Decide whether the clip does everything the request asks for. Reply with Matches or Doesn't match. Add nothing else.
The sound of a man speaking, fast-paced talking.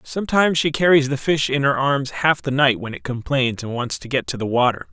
Matches